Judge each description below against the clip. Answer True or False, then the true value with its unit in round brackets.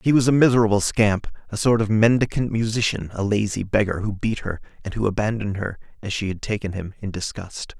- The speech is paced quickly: True (210 wpm)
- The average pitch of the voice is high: False (105 Hz)